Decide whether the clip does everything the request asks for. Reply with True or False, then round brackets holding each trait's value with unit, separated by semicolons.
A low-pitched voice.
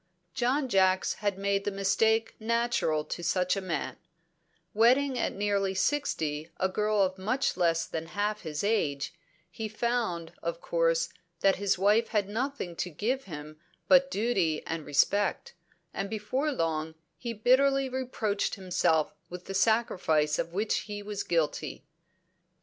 False (200 Hz)